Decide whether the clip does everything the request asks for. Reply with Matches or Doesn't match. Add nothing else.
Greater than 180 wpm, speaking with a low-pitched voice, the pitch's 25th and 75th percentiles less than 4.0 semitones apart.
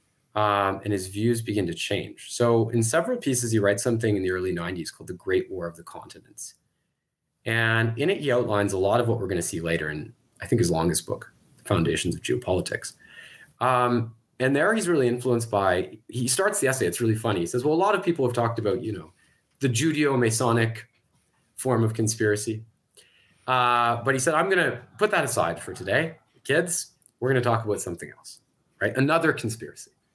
Matches